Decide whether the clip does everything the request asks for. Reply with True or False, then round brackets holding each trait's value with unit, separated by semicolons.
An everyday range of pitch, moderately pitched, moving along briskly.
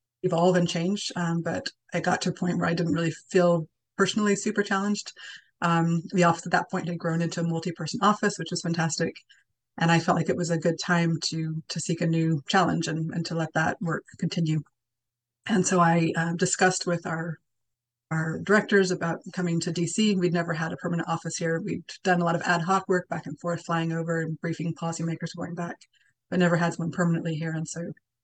False (1.5 semitones; 170 Hz; 215 wpm)